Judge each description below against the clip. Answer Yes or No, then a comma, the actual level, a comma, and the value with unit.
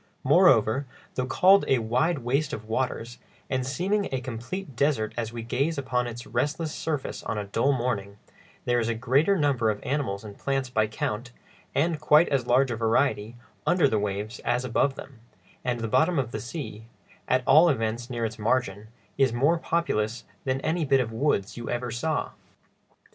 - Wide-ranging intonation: No, average, 3.9 semitones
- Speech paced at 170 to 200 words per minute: Yes, average, 175 wpm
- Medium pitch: No, low, 125 Hz